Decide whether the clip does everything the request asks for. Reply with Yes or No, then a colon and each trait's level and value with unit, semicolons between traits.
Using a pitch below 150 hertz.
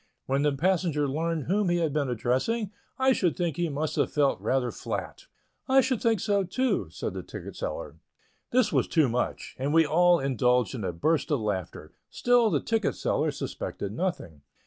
No: medium, 160 Hz